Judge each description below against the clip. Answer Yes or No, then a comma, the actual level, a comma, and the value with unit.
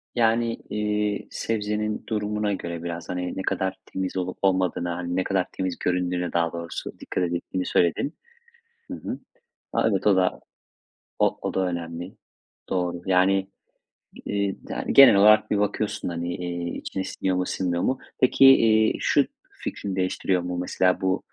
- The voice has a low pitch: Yes, very low, 95 Hz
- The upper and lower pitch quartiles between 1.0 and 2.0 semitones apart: No, average, 2.8 semitones